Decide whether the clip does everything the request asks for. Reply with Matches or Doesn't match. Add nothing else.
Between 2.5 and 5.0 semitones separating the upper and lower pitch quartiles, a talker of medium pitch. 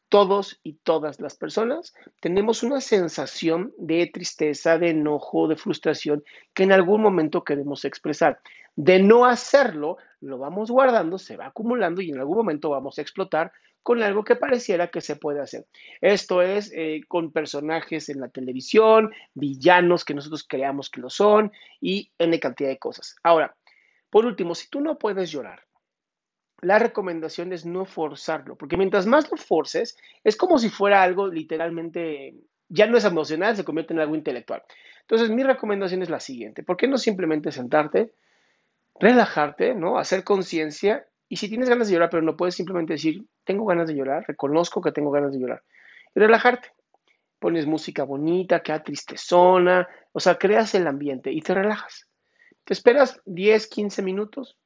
Doesn't match